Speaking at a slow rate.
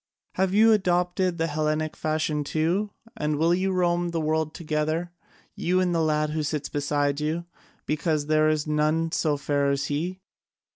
No: average, 165 wpm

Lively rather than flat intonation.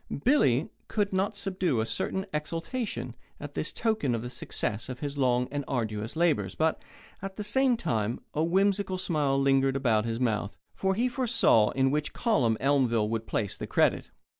Yes: wide, 8.4 semitones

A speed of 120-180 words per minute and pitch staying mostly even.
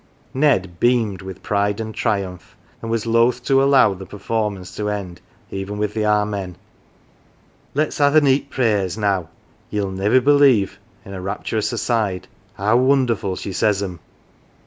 No: average, 175 wpm; average, 3.8 semitones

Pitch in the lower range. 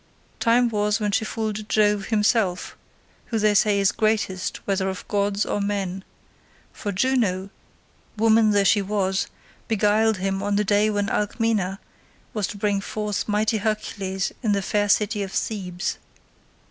No: high, 205 Hz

